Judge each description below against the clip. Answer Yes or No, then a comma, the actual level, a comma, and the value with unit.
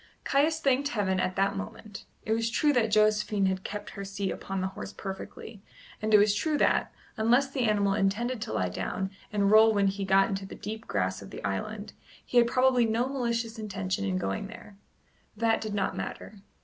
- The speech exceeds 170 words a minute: Yes, average, 200 wpm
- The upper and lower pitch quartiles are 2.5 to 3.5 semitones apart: Yes, average, 2.9 semitones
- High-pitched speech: Yes, high, 210 Hz